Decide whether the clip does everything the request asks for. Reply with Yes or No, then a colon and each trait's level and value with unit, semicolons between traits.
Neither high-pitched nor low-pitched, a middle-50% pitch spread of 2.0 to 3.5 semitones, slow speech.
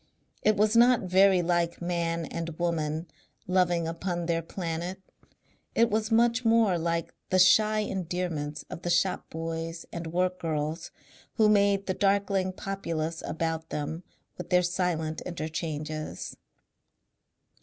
Yes: medium, 175 Hz; average, 3.0 semitones; slow, 130 wpm